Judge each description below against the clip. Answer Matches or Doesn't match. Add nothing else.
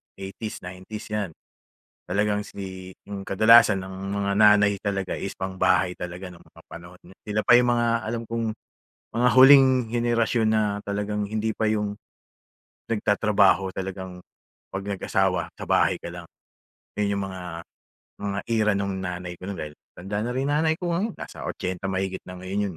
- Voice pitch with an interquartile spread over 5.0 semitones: Doesn't match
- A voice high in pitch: Doesn't match